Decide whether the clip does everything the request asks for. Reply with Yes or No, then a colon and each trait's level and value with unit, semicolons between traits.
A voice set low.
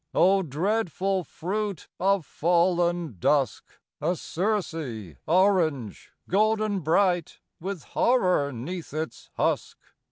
No: medium, 175 Hz